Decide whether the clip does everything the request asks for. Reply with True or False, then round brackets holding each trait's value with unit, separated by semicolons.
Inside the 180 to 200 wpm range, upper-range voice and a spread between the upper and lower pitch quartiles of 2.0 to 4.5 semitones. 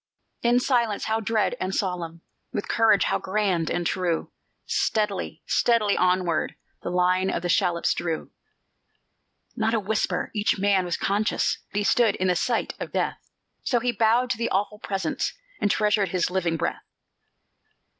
False (155 wpm; 200 Hz; 3.4 semitones)